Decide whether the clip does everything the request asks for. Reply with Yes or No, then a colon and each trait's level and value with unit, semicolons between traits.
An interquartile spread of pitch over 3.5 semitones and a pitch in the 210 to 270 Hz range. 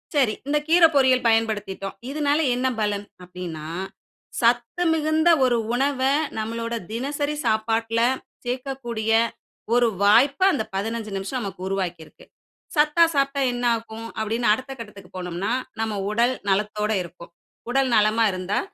Yes: average, 4.2 semitones; high, 230 Hz